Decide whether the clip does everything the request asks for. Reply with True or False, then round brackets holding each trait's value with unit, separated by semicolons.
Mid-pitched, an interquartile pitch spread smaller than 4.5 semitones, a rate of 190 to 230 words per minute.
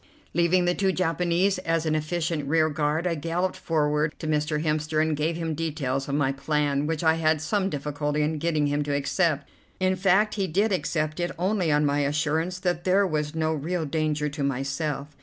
True (155 Hz; 2.7 semitones; 195 wpm)